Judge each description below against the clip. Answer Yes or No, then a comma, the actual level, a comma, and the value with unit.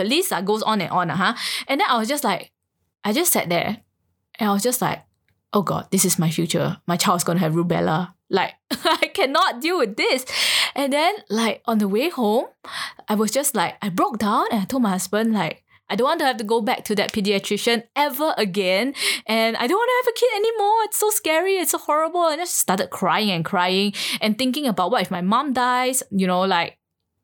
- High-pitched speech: Yes, high, 225 Hz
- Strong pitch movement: Yes, wide, 7.2 semitones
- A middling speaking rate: No, fast, 230 wpm